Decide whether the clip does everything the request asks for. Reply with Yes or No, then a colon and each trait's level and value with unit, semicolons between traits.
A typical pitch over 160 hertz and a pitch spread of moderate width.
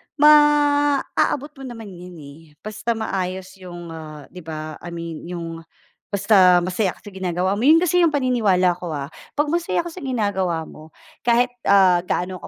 No: high, 190 Hz; wide, 6.7 semitones